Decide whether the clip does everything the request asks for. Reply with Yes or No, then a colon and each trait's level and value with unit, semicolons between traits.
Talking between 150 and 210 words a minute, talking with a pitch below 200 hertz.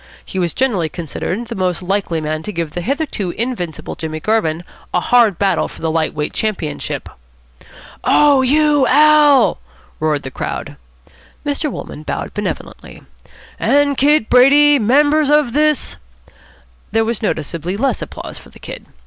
No: average, 155 wpm; high, 215 Hz